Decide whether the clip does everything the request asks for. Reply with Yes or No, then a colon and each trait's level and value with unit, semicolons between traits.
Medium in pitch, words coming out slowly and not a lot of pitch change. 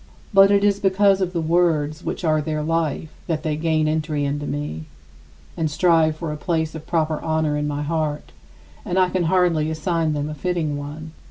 No: medium, 160 Hz; average, 195 wpm; narrow, 2.3 semitones